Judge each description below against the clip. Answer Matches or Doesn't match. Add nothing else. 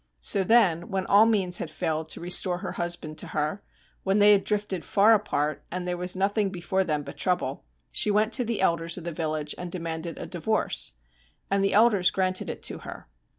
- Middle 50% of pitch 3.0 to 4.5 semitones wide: Matches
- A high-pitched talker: Doesn't match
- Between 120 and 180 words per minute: Doesn't match